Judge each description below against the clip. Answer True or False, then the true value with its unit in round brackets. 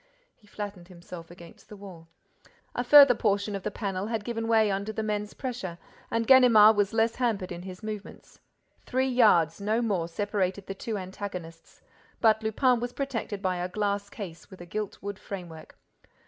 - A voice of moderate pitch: False (205 Hz)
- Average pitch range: True (3.3 semitones)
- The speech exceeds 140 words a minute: True (175 wpm)